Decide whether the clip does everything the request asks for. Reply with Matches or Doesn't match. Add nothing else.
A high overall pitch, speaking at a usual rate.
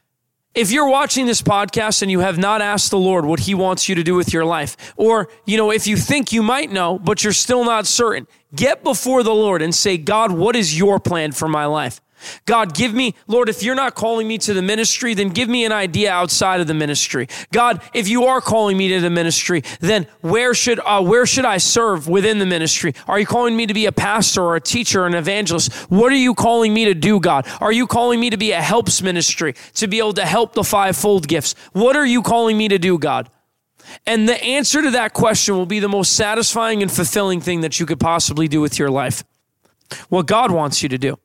Doesn't match